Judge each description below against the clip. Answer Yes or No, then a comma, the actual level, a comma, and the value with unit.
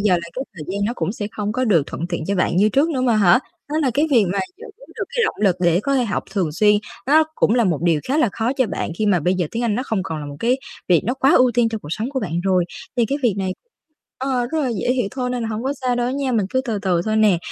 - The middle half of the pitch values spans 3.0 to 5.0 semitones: No, wide, 5.4 semitones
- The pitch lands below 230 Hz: Yes, high, 220 Hz